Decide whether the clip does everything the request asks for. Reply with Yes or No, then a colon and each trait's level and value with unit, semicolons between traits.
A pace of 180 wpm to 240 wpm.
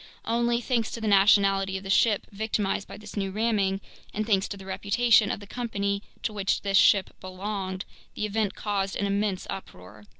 Yes: average, 190 wpm